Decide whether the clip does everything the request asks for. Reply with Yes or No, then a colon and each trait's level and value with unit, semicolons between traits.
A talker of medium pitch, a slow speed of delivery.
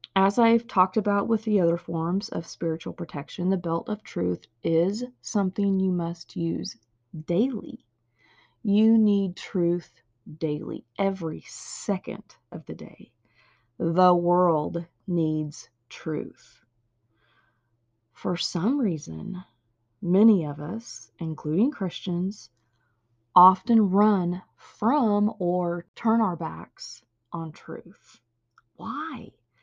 Yes: medium, 175 Hz; slow, 105 wpm